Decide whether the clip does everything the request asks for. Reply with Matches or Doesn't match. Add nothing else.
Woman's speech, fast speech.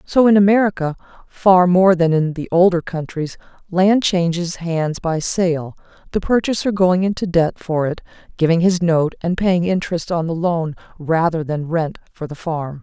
Doesn't match